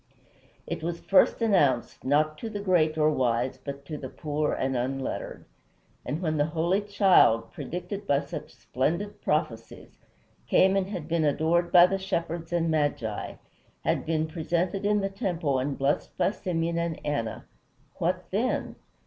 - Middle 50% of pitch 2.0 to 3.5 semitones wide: No, average, 4.1 semitones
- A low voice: No, medium, 160 Hz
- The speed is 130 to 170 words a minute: Yes, average, 155 wpm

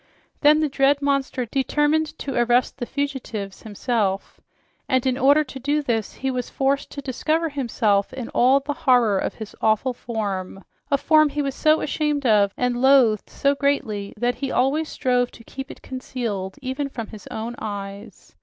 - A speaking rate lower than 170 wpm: No, average, 175 wpm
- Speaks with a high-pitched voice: Yes, very high, 260 Hz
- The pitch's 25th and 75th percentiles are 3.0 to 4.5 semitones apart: Yes, average, 4.1 semitones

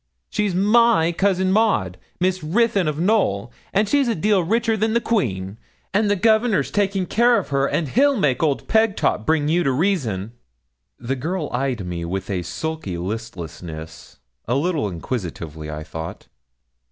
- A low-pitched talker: No, medium, 160 Hz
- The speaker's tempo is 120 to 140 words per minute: No, average, 160 wpm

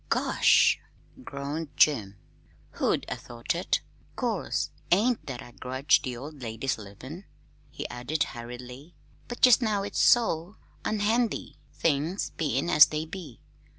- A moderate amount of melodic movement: No, wide, 7.1 semitones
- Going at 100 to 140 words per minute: Yes, slow, 135 wpm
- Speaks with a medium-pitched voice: Yes, medium, 150 Hz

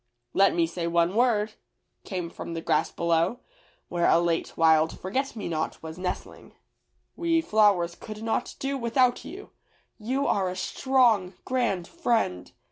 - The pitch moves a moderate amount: No, wide, 6.2 semitones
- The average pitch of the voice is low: No, high, 195 Hz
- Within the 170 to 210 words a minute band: No, average, 150 wpm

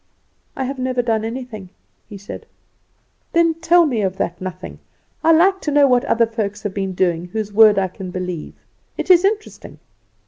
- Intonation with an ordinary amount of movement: No, wide, 7.0 semitones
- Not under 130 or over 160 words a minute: No, average, 180 wpm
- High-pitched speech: Yes, high, 225 Hz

